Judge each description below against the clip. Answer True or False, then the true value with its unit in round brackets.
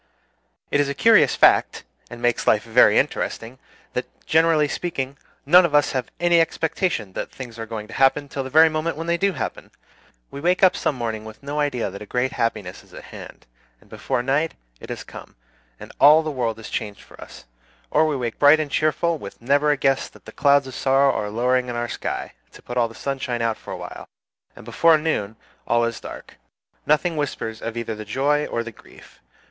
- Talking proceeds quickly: True (215 wpm)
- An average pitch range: True (4.8 semitones)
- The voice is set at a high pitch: False (135 Hz)